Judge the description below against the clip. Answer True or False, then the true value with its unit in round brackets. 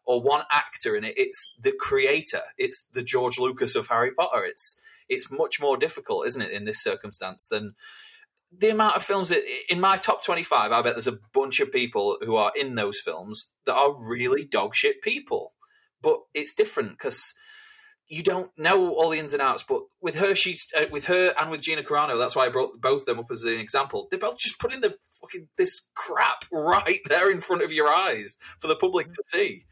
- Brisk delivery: True (210 wpm)